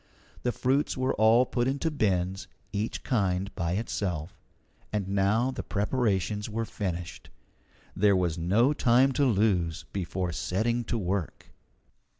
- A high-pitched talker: No, low, 105 Hz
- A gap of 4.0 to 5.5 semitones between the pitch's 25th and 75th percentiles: Yes, average, 4.6 semitones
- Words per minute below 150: Yes, slow, 135 wpm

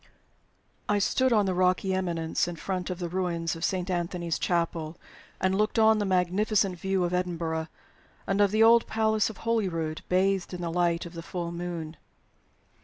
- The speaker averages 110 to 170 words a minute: No, average, 180 wpm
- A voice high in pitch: No, medium, 180 Hz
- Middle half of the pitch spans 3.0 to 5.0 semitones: No, narrow, 2.5 semitones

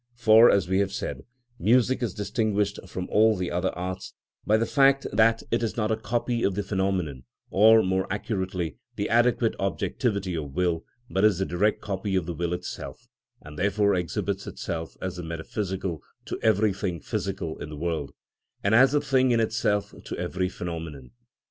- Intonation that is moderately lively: Yes, average, 3.8 semitones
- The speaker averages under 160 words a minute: No, average, 180 wpm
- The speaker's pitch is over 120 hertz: No, very low, 95 Hz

